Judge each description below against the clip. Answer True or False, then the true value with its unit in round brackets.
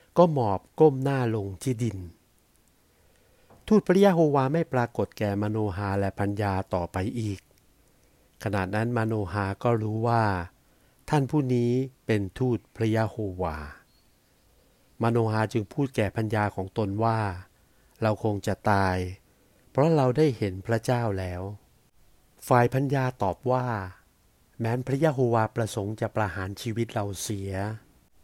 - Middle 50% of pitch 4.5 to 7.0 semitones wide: False (3.8 semitones)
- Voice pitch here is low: True (110 Hz)